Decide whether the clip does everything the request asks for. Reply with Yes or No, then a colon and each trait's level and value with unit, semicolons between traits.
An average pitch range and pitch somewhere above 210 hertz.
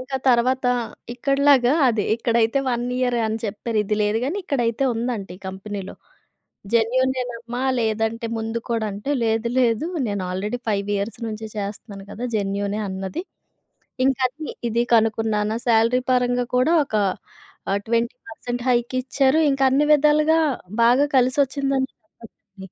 Yes: average, 3.0 semitones; high, 235 Hz